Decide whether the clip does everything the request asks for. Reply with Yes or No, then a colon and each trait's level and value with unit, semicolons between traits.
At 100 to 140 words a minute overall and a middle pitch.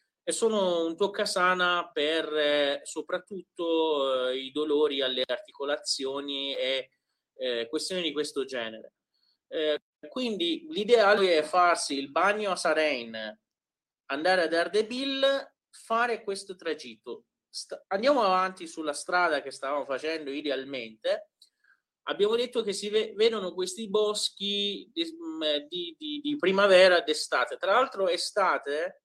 Yes: average, 125 wpm; medium, 180 Hz